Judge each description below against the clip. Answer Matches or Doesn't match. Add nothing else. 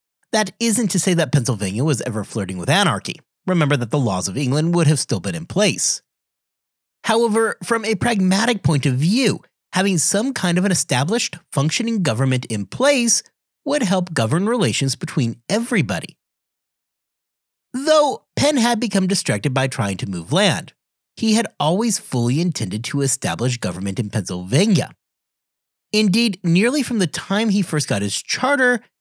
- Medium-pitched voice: Matches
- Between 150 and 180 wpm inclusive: Matches